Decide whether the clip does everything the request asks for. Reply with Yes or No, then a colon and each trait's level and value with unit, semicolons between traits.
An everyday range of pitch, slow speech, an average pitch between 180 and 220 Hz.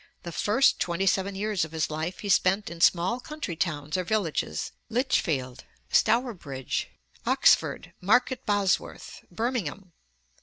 Yes: average, 4.9 semitones; slow, 125 wpm; medium, 185 Hz